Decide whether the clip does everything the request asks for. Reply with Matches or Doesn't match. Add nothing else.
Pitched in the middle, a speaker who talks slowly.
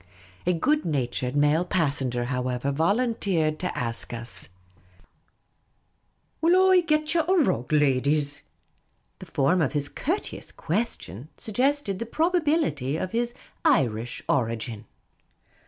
Matches